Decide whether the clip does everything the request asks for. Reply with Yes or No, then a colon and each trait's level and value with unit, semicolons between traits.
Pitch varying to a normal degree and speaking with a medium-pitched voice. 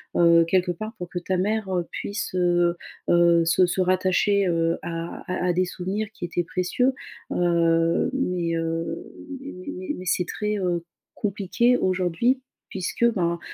No: narrow, 2.1 semitones; medium, 180 Hz